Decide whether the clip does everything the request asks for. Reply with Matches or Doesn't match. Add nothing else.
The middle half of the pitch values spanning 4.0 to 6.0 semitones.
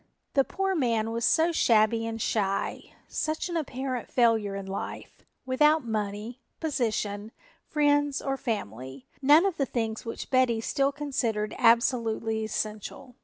Matches